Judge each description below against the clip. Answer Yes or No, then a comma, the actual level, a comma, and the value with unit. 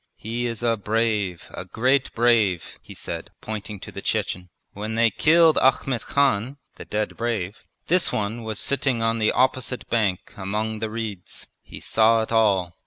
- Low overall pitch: Yes, low, 110 Hz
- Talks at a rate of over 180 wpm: No, average, 170 wpm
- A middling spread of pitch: No, narrow, 2.3 semitones